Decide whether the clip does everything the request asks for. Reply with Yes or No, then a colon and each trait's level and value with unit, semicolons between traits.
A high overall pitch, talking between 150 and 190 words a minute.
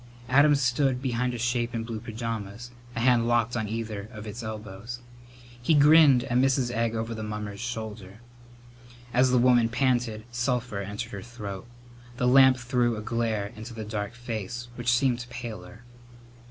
No: low, 120 Hz; average, 165 wpm